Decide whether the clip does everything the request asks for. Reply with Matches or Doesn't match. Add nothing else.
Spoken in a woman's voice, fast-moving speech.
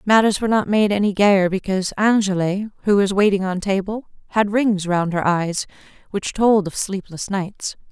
Doesn't match